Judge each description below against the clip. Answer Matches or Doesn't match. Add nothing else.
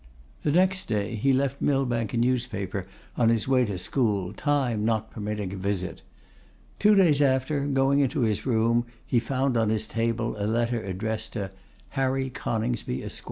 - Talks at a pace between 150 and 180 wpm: Matches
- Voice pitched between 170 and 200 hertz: Doesn't match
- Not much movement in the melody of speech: Doesn't match